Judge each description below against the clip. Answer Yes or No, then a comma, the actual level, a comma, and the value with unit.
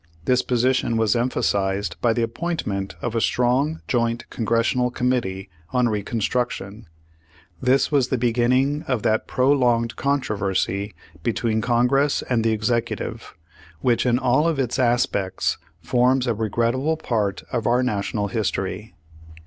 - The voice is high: No, low, 120 Hz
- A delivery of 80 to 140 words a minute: Yes, slow, 135 wpm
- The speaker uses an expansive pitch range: No, average, 2.7 semitones